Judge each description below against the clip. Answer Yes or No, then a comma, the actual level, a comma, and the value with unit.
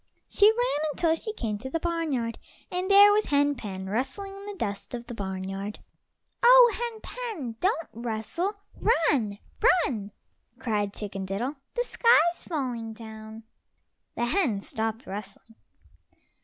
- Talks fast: No, slow, 135 wpm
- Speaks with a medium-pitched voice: No, very high, 265 Hz